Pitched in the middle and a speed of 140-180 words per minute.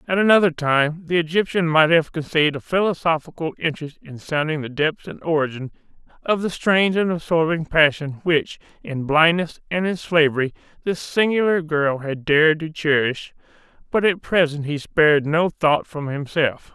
Yes: medium, 160 Hz; average, 160 wpm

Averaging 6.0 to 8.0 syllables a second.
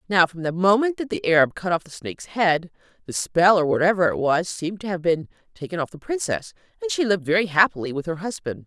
Yes: 6.2 syllables/s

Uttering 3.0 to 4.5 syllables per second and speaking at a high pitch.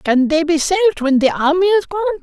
No: 6.1 syllables/s; very high, 280 Hz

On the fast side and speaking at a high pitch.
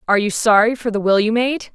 Yes: fast, 275 wpm; high, 220 Hz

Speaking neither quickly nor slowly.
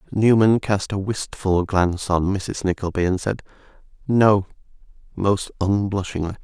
No: slow, 120 wpm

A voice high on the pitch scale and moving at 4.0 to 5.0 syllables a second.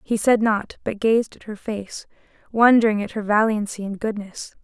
Yes: high, 215 Hz; 4.8 syllables/s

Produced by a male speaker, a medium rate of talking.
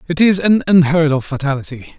Yes: male; average, 180 wpm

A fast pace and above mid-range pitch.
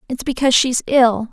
Yes: fast, 225 wpm; very high, 250 Hz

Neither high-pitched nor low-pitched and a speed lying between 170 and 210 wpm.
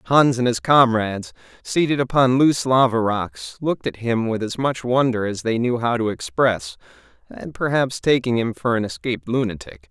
No: low, 120 Hz; average, 180 wpm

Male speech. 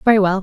No: female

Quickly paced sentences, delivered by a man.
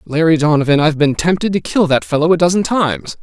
Yes: fast, 225 wpm; male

